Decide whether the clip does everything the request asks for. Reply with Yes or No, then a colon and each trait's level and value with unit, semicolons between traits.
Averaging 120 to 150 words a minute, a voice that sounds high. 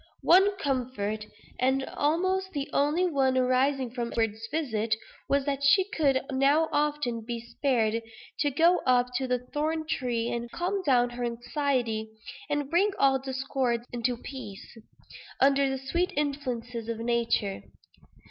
Yes: average, 140 wpm; very high, 265 Hz